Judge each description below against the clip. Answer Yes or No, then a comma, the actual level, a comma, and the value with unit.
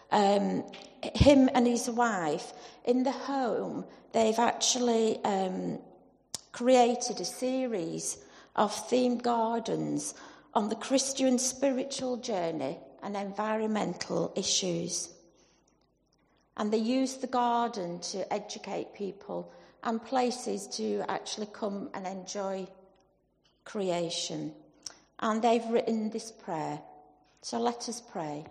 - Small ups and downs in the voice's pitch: No, average, 4.4 semitones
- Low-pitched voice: No, high, 220 Hz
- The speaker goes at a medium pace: No, slow, 105 wpm